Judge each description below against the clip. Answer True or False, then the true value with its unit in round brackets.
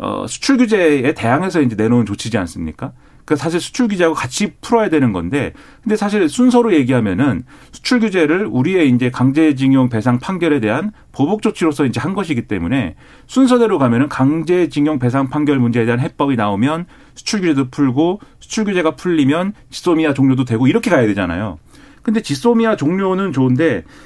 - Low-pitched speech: False (150 Hz)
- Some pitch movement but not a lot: False (7.3 semitones)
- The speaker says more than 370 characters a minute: True (395 characters per minute)